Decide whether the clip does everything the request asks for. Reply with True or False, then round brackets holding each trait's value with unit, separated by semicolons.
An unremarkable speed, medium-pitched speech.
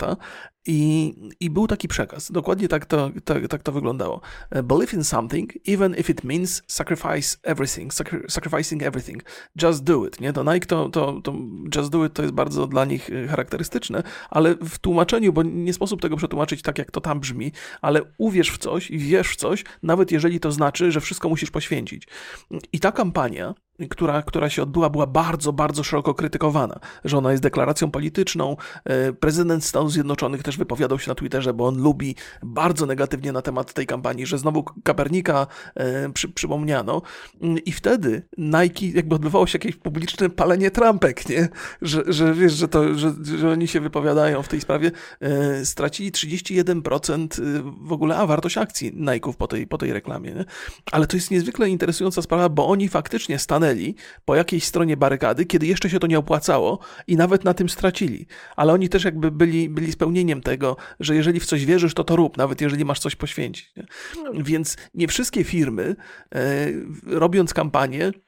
False (175 wpm; 160 Hz)